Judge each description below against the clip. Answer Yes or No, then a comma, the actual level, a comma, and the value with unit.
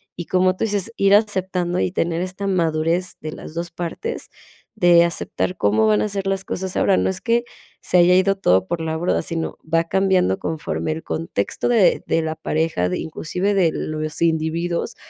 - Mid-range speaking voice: Yes, medium, 175 Hz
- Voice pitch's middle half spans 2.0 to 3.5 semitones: Yes, average, 3.0 semitones